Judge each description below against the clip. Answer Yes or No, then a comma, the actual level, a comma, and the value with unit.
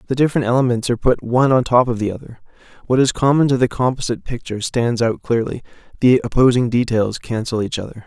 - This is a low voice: Yes, low, 120 Hz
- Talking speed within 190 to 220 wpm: Yes, average, 200 wpm